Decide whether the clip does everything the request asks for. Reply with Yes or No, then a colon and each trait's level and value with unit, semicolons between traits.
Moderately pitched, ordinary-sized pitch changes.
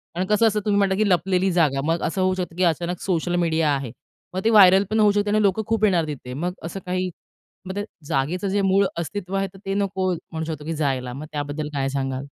Yes: medium, 180 Hz; average, 4.1 semitones